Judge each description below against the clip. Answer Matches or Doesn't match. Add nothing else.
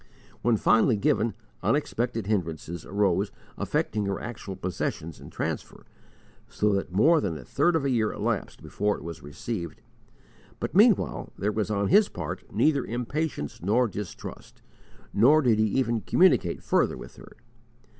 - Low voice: Matches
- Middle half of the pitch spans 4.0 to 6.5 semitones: Matches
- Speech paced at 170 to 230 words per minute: Doesn't match